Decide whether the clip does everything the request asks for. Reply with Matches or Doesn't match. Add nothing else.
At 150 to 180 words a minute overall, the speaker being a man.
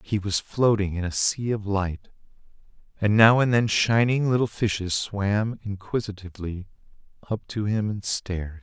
Matches